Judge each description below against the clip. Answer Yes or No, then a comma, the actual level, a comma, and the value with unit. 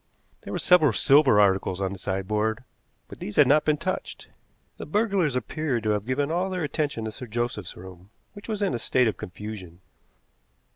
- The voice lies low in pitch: Yes, low, 120 Hz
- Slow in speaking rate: No, average, 190 wpm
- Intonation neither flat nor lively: No, wide, 6.7 semitones